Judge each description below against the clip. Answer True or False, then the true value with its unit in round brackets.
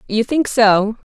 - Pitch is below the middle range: False (225 Hz)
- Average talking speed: True (160 wpm)